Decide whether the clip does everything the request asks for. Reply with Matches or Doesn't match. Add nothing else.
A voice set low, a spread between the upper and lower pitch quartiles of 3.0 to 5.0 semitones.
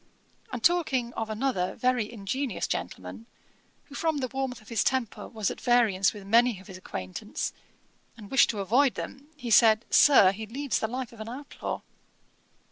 Doesn't match